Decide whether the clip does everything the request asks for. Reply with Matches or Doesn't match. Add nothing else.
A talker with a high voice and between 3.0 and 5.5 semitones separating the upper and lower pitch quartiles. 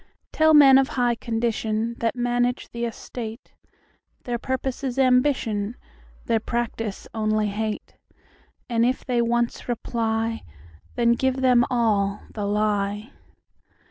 Doesn't match